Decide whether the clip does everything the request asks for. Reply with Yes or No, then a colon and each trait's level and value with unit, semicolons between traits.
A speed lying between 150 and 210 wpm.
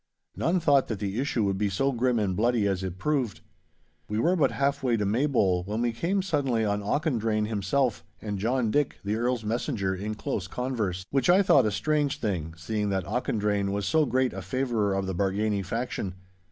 Yes: average, 195 wpm